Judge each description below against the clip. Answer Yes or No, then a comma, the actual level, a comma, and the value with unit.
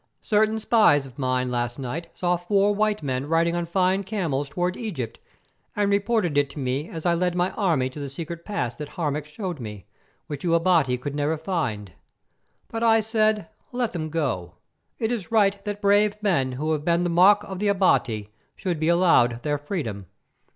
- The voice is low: No, medium, 170 Hz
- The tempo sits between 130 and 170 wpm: No, average, 190 wpm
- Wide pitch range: Yes, wide, 6.3 semitones